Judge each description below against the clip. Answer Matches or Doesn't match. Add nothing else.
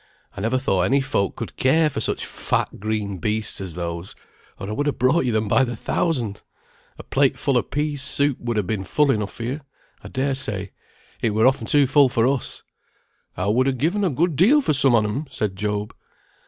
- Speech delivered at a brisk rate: Matches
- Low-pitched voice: Matches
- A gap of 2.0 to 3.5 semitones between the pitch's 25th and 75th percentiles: Doesn't match